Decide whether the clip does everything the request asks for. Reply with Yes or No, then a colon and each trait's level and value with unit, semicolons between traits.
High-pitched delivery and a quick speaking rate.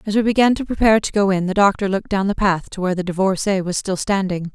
Yes: high, 195 Hz; fast, 275 wpm